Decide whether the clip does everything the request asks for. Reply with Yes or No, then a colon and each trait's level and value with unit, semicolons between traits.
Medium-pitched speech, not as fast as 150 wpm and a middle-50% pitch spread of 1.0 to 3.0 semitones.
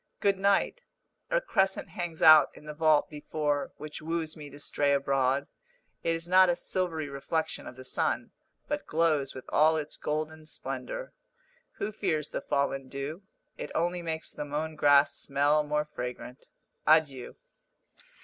No: medium, 155 Hz; average, 155 wpm; average, 2.7 semitones